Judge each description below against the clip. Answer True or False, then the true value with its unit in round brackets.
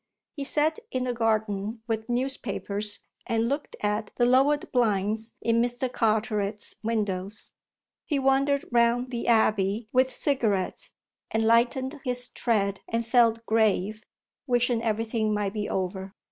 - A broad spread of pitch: False (2.8 semitones)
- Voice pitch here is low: False (230 Hz)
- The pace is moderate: False (130 wpm)